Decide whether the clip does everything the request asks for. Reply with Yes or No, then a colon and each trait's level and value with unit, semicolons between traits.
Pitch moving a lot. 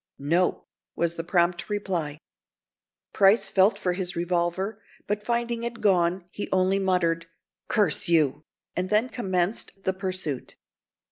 No: average, 3.1 semitones